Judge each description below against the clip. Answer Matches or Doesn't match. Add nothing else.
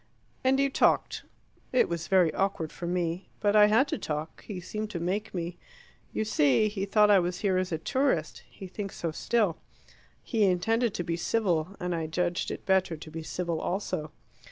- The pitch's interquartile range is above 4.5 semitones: Doesn't match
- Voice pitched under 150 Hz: Doesn't match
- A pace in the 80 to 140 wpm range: Doesn't match